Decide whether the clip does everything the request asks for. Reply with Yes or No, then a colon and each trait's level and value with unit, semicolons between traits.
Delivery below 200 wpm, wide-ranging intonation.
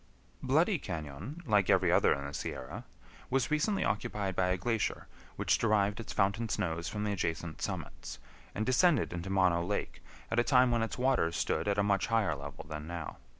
Yes: average, 190 wpm; wide, 5.7 semitones